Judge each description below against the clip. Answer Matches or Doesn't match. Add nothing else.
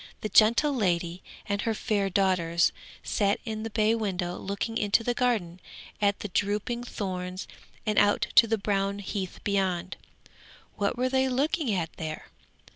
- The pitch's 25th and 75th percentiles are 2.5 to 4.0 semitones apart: Matches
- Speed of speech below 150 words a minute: Doesn't match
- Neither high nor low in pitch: Doesn't match